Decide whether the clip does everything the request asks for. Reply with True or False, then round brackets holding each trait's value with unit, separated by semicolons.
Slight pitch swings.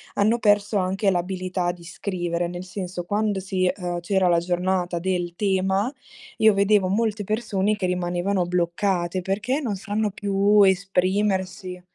True (2.3 semitones)